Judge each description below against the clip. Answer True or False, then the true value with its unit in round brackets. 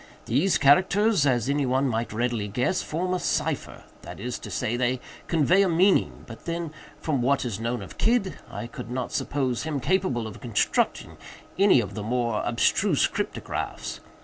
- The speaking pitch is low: True (130 Hz)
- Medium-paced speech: True (170 wpm)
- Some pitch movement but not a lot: False (6.1 semitones)